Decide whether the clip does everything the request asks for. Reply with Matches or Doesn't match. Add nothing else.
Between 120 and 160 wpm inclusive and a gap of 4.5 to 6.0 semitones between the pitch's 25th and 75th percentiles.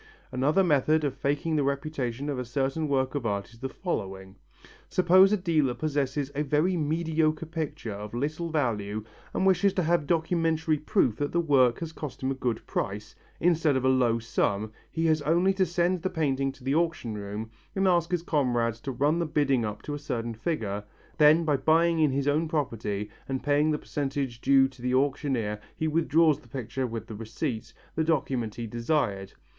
Doesn't match